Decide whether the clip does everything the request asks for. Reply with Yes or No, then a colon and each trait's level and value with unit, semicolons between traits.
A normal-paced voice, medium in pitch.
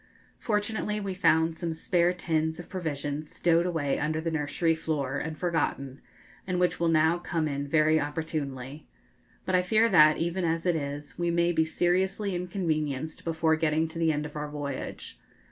Yes: average, 175 wpm; medium, 160 Hz